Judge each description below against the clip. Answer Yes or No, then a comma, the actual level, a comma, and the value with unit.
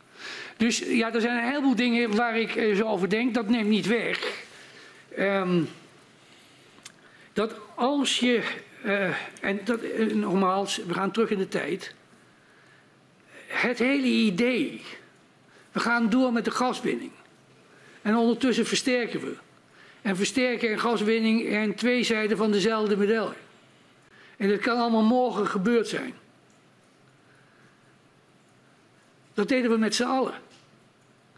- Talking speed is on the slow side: Yes, slow, 130 wpm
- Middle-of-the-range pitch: No, high, 225 Hz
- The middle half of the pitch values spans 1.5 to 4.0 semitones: Yes, narrow, 2.5 semitones